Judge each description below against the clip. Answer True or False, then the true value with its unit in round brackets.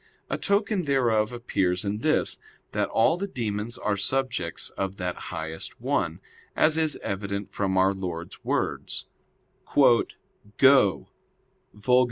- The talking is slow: True (125 wpm)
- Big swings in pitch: True (5.8 semitones)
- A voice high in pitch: False (105 Hz)